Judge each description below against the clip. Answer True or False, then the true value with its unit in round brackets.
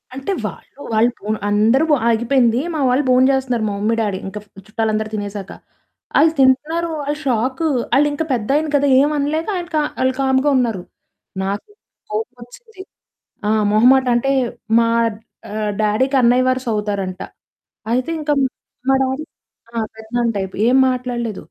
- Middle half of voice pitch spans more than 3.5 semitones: True (4.0 semitones)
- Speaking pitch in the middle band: False (250 Hz)